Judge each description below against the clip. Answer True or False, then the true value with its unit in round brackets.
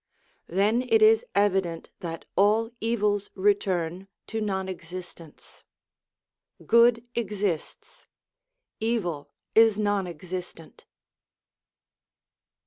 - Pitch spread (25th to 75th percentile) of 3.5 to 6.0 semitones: True (3.9 semitones)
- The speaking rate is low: True (80 wpm)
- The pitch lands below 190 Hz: False (200 Hz)